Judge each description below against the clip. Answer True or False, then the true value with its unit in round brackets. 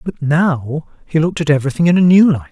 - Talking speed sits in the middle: False (240 wpm)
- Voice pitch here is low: False (155 Hz)